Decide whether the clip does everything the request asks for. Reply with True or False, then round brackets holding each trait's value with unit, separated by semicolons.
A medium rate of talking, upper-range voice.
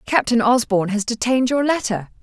True (160 wpm; 235 Hz)